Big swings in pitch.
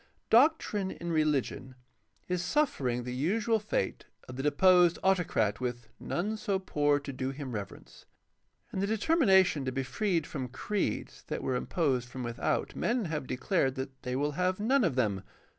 Yes: wide, 6.9 semitones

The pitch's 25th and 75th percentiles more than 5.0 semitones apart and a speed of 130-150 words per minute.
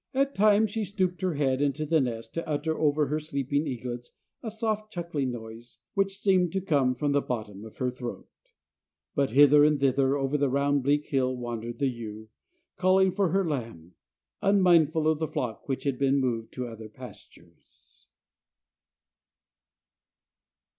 No: wide, 5.4 semitones; average, 160 wpm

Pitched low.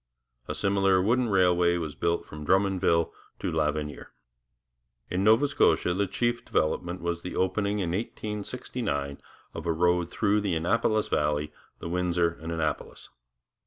Yes: very low, 90 Hz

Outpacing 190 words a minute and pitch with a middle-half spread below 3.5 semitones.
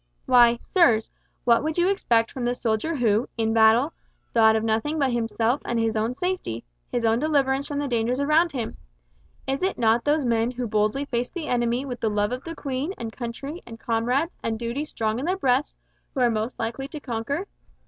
No: average, 200 wpm; average, 3.8 semitones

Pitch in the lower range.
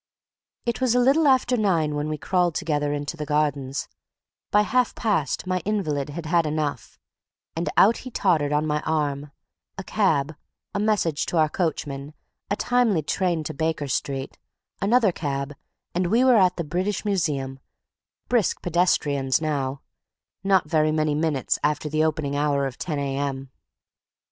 No: medium, 155 Hz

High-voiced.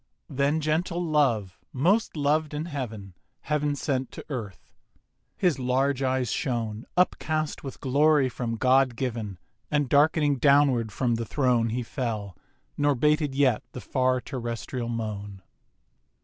No: low, 130 Hz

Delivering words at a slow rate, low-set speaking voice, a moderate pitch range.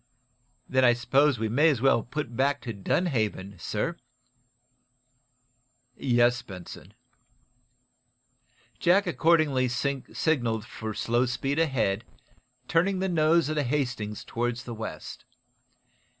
Yes: slow, 110 wpm; low, 125 Hz; average, 4.8 semitones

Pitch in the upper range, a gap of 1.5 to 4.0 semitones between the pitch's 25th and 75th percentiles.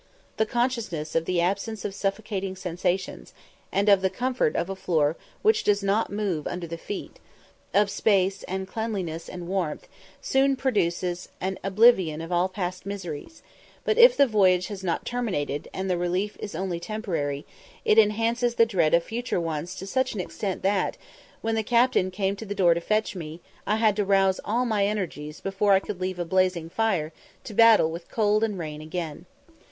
Yes: high, 195 Hz; average, 3.6 semitones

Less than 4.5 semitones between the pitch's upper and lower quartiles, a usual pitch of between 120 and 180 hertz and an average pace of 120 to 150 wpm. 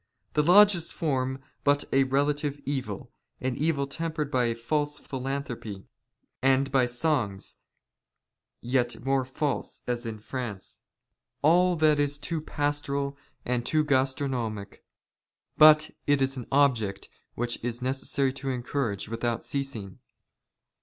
Yes: average, 3.2 semitones; low, 135 Hz; slow, 135 wpm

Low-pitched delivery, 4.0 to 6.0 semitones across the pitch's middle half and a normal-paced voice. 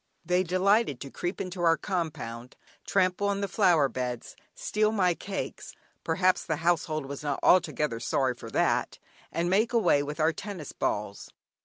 No: medium, 170 Hz; average, 4.8 semitones; average, 160 wpm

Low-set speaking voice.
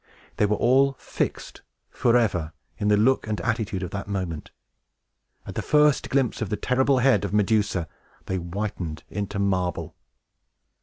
Yes: low, 105 Hz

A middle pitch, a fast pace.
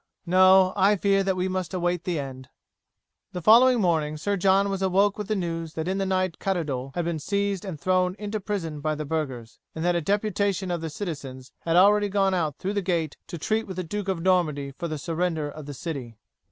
Yes: medium, 180 Hz; fast, 220 wpm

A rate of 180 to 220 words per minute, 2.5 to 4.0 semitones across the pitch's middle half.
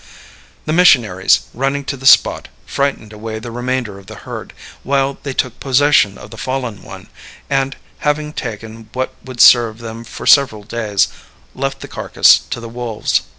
No: average, 165 wpm; average, 3.7 semitones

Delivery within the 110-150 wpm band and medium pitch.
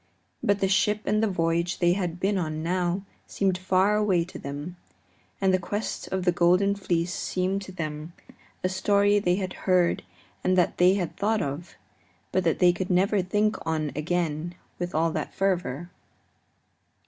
No: average, 170 wpm; medium, 180 Hz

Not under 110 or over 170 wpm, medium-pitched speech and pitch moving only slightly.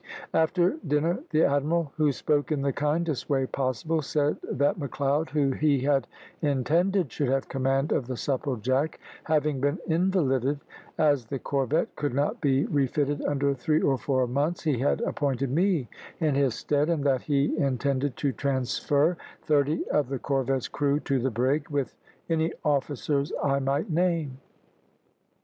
Yes: average, 155 wpm; medium, 145 Hz; narrow, 2.3 semitones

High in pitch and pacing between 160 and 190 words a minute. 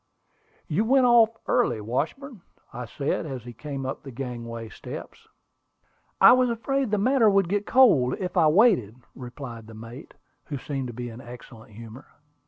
No: medium, 140 Hz; average, 170 wpm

